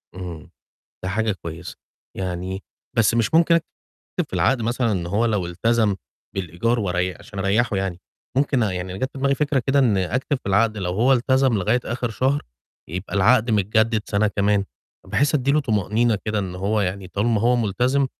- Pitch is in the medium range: No, low, 110 Hz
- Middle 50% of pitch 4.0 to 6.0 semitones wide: Yes, average, 4.5 semitones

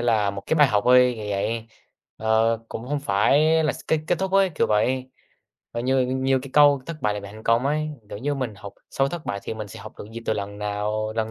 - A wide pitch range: No, average, 4.9 semitones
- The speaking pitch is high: No, low, 120 Hz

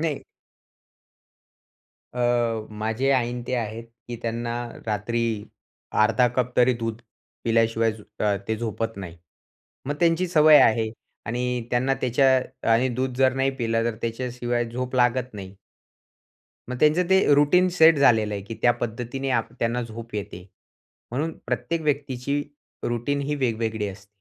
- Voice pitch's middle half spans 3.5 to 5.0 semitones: No, average, 2.9 semitones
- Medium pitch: No, low, 120 Hz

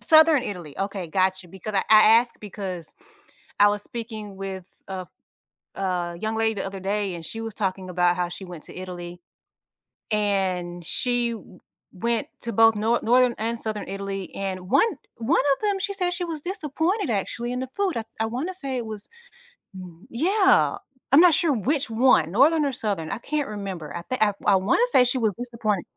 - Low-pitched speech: No, high, 215 Hz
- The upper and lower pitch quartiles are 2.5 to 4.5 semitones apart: No, average, 5.0 semitones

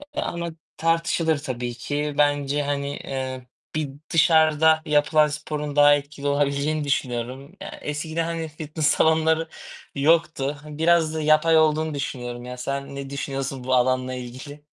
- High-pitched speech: No, medium, 145 Hz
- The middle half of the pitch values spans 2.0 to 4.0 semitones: Yes, narrow, 2.4 semitones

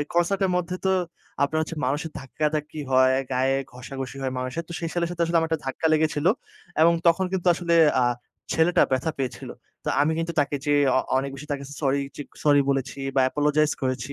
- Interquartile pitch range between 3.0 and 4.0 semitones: Yes, average, 3.7 semitones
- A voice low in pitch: No, medium, 150 Hz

